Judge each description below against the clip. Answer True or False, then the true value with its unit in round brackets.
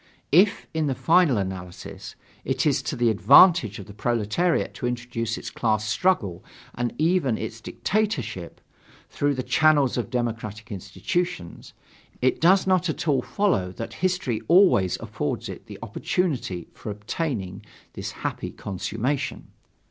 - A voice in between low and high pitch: False (120 Hz)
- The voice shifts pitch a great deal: True (7.7 semitones)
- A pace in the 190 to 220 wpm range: False (140 wpm)